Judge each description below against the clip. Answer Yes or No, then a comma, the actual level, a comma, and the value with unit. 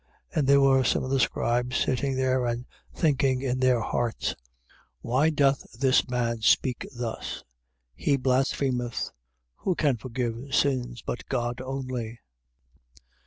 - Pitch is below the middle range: Yes, low, 130 Hz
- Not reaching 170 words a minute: Yes, average, 140 wpm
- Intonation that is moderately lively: No, narrow, 2.0 semitones